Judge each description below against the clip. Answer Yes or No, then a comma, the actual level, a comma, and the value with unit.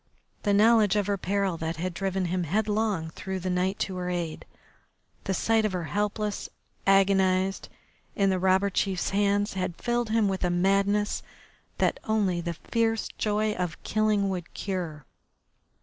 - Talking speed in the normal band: Yes, average, 160 wpm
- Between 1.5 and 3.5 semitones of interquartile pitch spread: Yes, narrow, 2.4 semitones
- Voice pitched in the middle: No, high, 195 Hz